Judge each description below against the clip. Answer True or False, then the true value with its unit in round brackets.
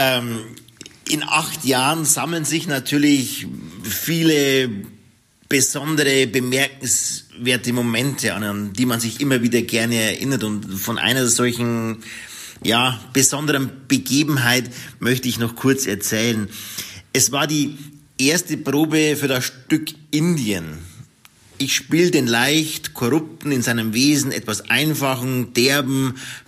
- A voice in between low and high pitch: False (130 Hz)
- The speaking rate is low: True (115 wpm)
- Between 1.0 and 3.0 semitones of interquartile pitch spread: False (3.8 semitones)